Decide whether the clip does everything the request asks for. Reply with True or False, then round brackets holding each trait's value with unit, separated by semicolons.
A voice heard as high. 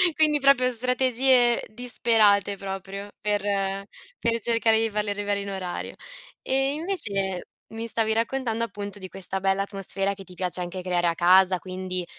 True (205 Hz)